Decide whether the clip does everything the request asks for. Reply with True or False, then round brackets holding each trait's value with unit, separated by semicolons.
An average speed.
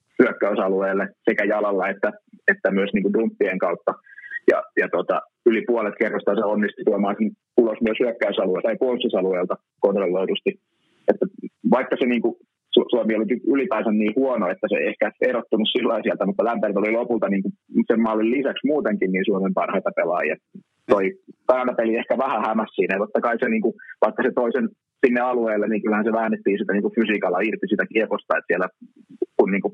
False (175 wpm)